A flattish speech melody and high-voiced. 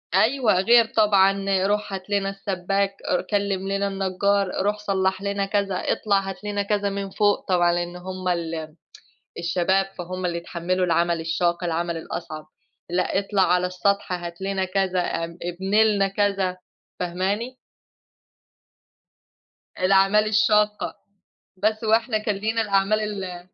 Yes: narrow, 2.2 semitones; high, 195 Hz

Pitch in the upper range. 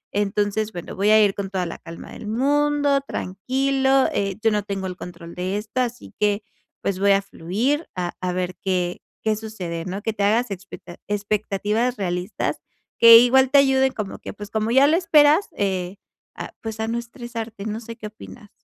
Yes: high, 210 Hz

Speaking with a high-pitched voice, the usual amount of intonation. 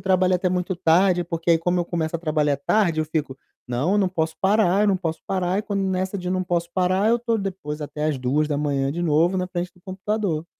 No: medium, 175 Hz; average, 3.2 semitones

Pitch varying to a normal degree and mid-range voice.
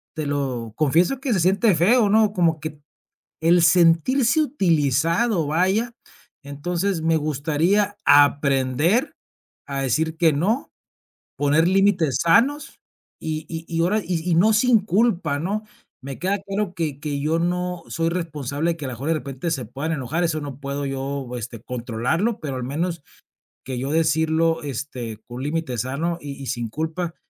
Yes: average, 4.2 semitones; medium, 160 Hz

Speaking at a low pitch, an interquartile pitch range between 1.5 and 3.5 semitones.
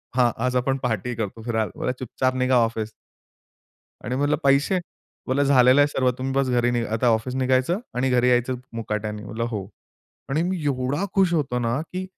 Yes: low, 125 Hz; narrow, 2.6 semitones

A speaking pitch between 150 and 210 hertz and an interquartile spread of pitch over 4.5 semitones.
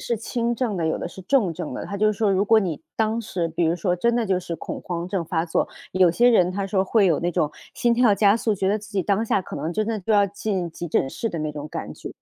No: high, 195 Hz; average, 4.0 semitones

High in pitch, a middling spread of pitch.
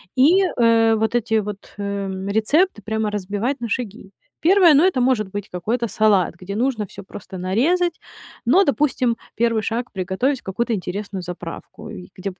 Yes: high, 220 Hz; average, 4.2 semitones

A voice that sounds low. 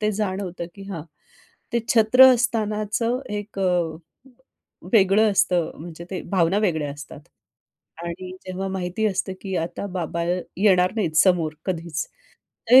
No: medium, 185 Hz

